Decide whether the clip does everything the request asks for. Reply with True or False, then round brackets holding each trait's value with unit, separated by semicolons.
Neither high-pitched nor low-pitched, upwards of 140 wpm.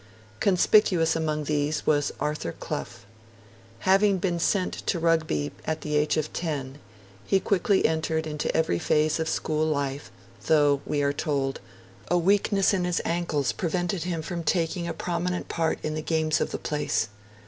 True (160 Hz; 160 wpm)